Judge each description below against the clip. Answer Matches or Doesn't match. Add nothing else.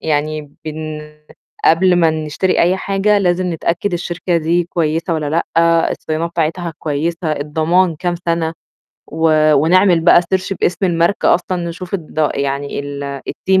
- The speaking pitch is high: Doesn't match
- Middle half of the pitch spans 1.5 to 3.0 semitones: Matches